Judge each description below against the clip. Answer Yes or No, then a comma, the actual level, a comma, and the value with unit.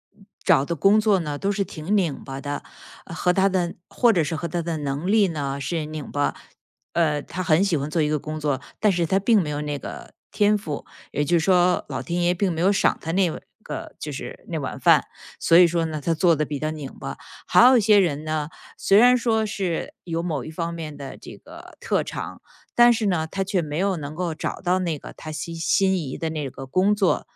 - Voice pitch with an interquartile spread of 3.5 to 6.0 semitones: Yes, average, 4.0 semitones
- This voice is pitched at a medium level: Yes, medium, 170 Hz